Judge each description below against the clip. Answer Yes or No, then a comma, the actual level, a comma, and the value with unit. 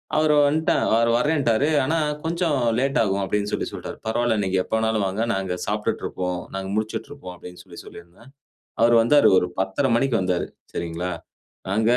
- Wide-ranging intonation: Yes, wide, 6.2 semitones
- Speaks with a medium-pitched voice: No, low, 110 Hz